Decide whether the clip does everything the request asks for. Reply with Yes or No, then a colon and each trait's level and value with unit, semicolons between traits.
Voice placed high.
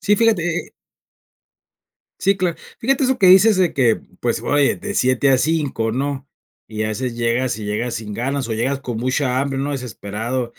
No: low, 130 Hz